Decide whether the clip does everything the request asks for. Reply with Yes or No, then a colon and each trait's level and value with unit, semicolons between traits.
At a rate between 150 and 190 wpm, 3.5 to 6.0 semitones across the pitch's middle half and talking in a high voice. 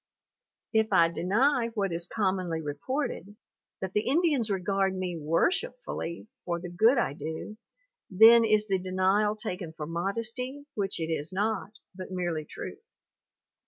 No: average, 140 wpm; average, 4.3 semitones; high, 195 Hz